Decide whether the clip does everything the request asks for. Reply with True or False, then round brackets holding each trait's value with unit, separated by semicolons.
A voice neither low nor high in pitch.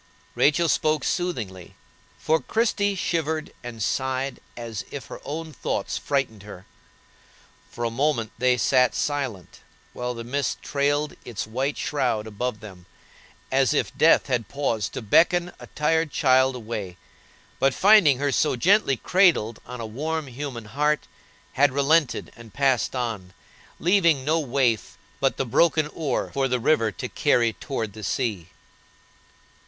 False (130 Hz)